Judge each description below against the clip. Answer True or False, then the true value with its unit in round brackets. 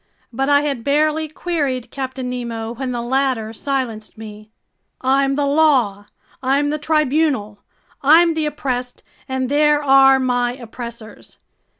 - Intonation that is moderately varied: True (3.3 semitones)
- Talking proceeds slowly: True (130 wpm)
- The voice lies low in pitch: False (265 Hz)